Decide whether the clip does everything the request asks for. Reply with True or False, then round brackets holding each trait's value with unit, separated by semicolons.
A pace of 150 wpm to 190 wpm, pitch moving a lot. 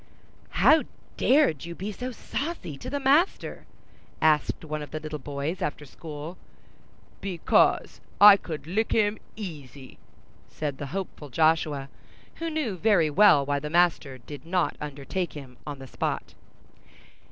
False (140 wpm; 5.8 semitones)